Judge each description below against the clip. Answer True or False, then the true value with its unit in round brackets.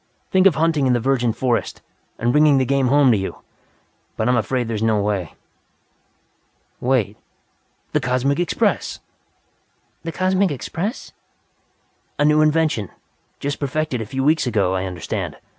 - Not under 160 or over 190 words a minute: False (150 wpm)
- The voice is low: True (130 Hz)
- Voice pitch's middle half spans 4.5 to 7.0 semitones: True (5.3 semitones)